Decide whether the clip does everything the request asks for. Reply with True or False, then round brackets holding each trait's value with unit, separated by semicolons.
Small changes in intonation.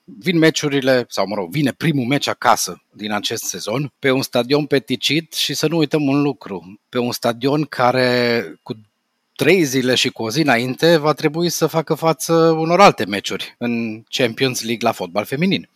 False (4.6 semitones)